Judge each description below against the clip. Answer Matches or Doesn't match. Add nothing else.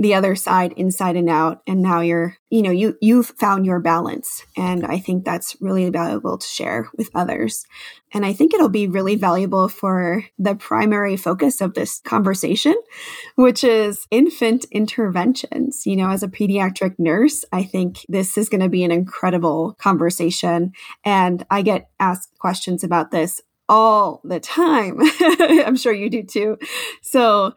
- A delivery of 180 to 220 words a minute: Doesn't match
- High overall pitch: Matches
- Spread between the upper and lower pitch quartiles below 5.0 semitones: Matches